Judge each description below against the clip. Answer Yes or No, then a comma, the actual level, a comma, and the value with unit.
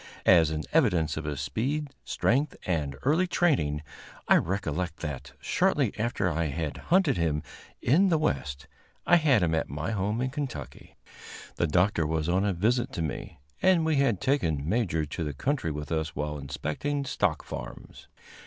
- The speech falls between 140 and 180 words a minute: Yes, average, 170 wpm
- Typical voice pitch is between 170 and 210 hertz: No, very low, 90 Hz